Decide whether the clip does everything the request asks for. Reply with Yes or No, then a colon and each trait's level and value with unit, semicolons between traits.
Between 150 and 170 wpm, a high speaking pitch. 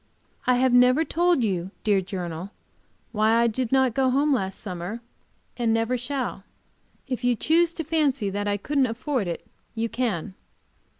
Yes: average, 165 wpm; high, 240 Hz